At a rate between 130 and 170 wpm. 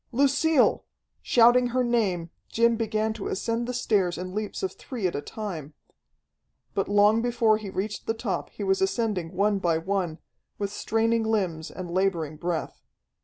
Yes: average, 165 wpm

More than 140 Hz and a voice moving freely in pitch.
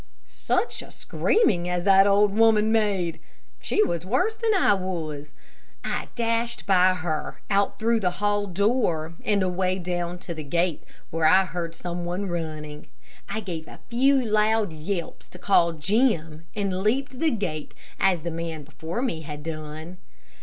No: medium, 185 Hz; average, 4.4 semitones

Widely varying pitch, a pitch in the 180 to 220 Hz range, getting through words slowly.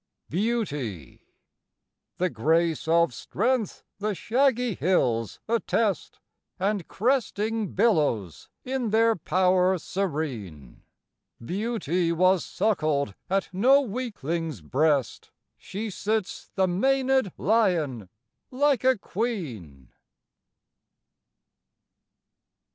Yes: wide, 6.9 semitones; medium, 185 Hz; slow, 80 wpm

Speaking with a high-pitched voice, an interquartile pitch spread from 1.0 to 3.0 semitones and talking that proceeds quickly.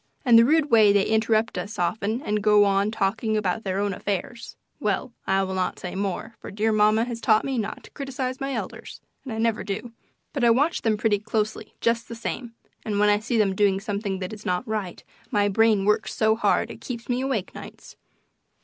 Yes: high, 215 Hz; narrow, 2.4 semitones; fast, 215 wpm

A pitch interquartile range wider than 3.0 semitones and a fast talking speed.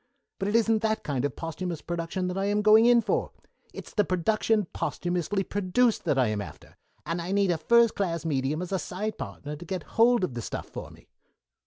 Yes: average, 4.5 semitones; fast, 215 wpm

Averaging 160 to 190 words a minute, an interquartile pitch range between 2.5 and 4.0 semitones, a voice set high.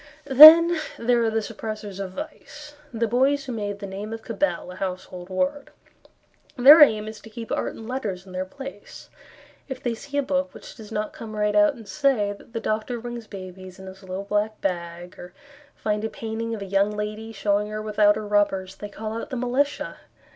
No: fast, 205 wpm; average, 3.7 semitones; high, 215 Hz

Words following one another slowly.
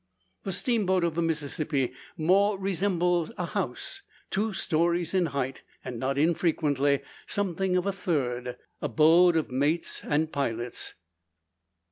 Yes: slow, 125 wpm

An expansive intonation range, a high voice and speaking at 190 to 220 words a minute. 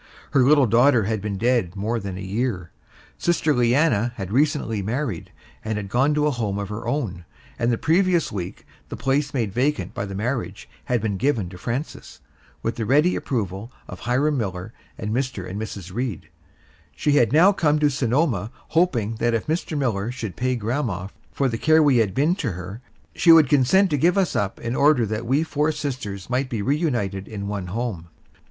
No: wide, 6.0 semitones; low, 120 Hz; average, 195 wpm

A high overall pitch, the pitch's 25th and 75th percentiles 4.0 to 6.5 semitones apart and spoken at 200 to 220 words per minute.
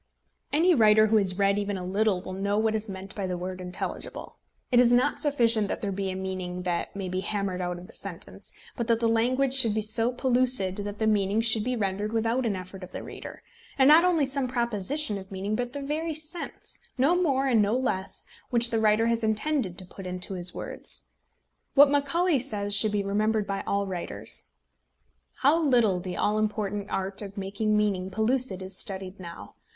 Yes: high, 215 Hz; average, 4.4 semitones; fast, 205 wpm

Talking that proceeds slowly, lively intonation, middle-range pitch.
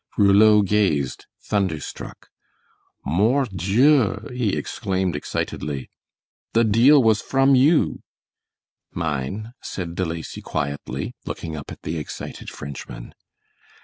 No: slow, 105 wpm; wide, 6.2 semitones; low, 100 Hz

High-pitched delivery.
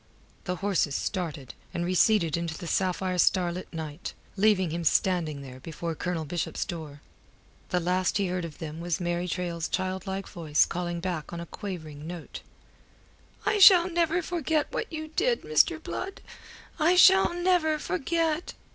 No: medium, 180 Hz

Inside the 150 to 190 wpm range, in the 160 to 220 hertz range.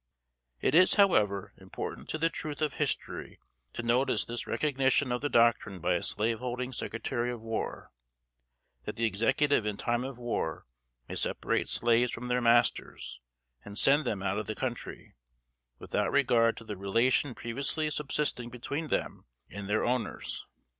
No: average, 160 wpm; low, 120 Hz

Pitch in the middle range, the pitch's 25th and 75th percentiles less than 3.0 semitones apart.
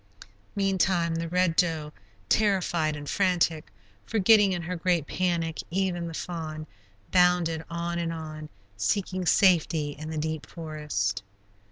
Yes: medium, 170 Hz; narrow, 2.6 semitones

